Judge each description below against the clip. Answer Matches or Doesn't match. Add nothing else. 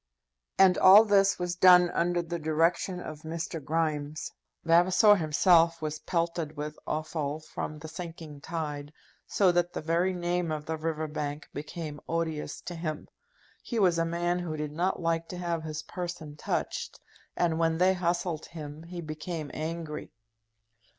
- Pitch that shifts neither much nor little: Doesn't match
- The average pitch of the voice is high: Doesn't match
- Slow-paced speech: Doesn't match